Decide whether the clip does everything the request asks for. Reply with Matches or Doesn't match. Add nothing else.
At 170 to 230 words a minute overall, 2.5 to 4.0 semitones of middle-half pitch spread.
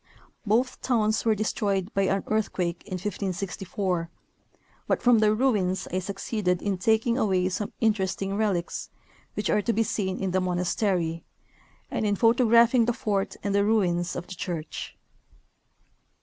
Doesn't match